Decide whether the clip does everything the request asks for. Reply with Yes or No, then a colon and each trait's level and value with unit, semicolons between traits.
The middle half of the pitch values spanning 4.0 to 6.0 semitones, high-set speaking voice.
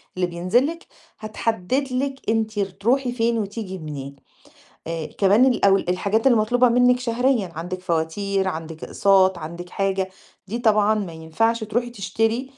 Yes: average, 4.6 semitones; high, 205 Hz